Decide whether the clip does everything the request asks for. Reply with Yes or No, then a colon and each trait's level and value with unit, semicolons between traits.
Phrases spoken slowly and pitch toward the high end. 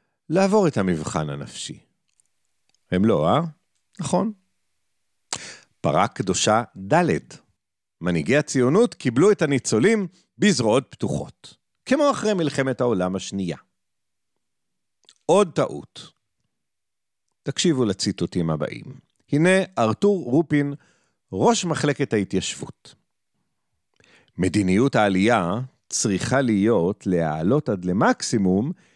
No: slow, 85 wpm; medium, 140 Hz